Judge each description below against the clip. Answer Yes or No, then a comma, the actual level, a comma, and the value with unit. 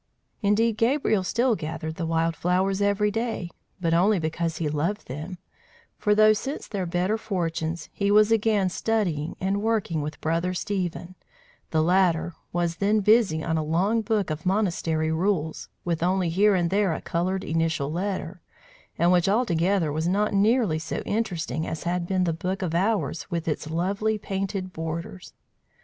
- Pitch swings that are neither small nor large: Yes, average, 3.9 semitones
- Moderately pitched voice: Yes, medium, 180 Hz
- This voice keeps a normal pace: Yes, average, 165 wpm